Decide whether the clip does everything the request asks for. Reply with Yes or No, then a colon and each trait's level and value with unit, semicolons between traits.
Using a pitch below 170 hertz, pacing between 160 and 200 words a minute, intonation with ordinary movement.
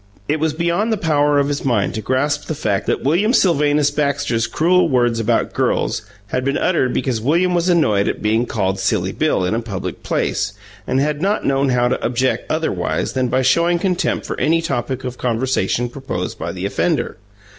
Yes: low, 135 Hz; average, 195 wpm; average, 4.7 semitones